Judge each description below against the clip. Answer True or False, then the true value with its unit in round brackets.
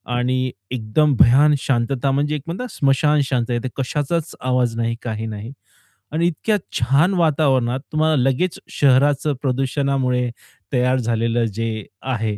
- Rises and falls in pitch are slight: False (3.7 semitones)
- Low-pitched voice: True (130 Hz)